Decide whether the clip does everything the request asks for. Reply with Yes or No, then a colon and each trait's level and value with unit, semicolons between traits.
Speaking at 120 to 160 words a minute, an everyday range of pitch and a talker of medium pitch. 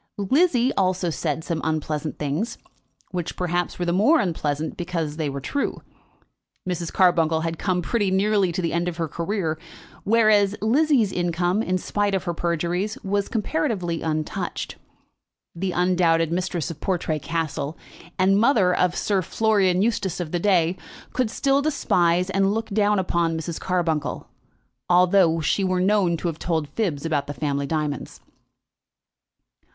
Yes: average, 155 wpm; average, 3.5 semitones; medium, 180 Hz